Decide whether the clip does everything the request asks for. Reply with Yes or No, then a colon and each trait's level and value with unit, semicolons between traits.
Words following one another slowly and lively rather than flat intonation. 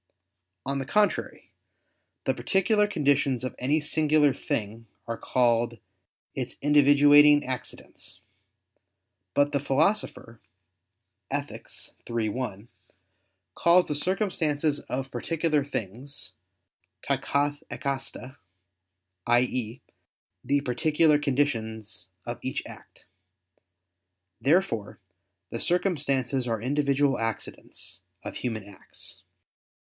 No: slow, 90 wpm; average, 3.7 semitones